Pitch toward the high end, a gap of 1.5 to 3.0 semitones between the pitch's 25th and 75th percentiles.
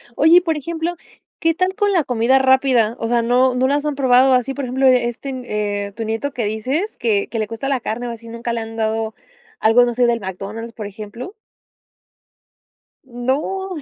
No: high, 245 Hz; average, 3.5 semitones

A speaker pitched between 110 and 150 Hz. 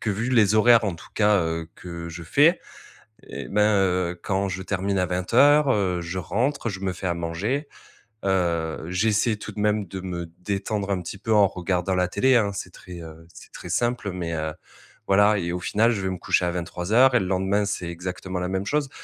No: very low, 95 Hz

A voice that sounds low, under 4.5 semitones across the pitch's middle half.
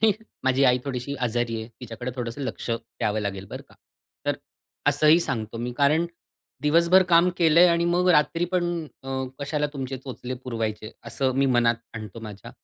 No: low, 130 Hz; average, 4.9 semitones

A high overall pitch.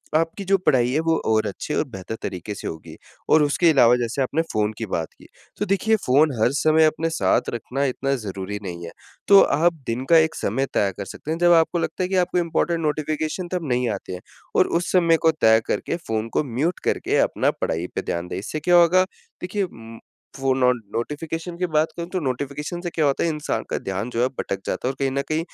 No: medium, 145 Hz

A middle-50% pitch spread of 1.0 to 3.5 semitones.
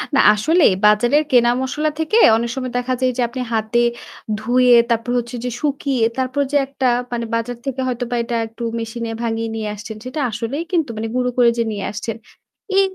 Yes: narrow, 2.4 semitones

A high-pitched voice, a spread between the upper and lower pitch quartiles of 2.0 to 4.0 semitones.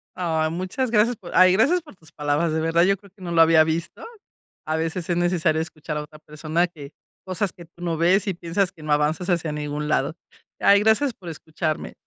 No: medium, 170 Hz; average, 2.9 semitones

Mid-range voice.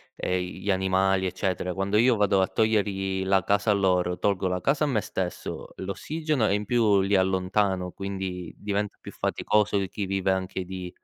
No: very low, 95 Hz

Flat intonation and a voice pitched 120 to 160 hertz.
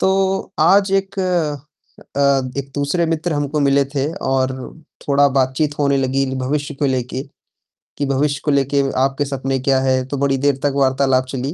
Yes: narrow, 2.0 semitones; medium, 140 Hz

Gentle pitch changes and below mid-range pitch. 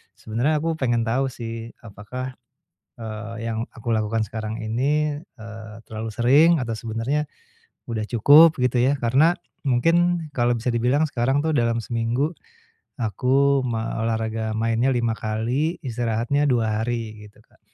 No: average, 3.4 semitones; low, 120 Hz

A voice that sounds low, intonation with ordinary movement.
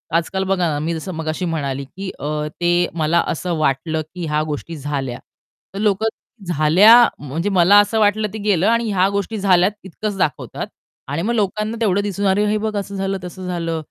No: medium, 185 Hz; average, 4.2 semitones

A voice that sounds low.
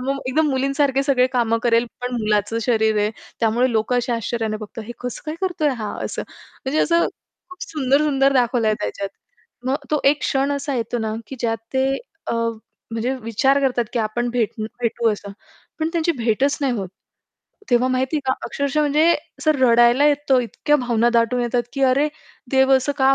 No: very high, 250 Hz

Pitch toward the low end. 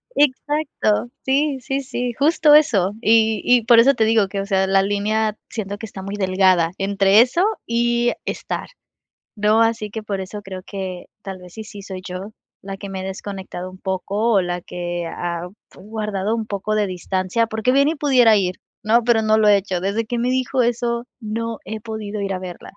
No: high, 210 Hz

